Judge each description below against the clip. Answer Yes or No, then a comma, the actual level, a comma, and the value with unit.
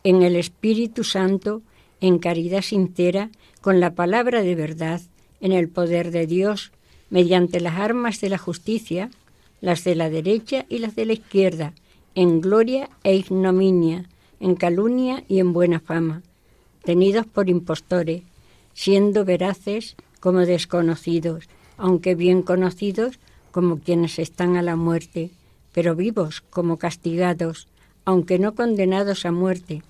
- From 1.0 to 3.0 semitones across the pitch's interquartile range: Yes, narrow, 2.5 semitones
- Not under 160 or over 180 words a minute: No, average, 135 wpm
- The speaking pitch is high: No, medium, 180 Hz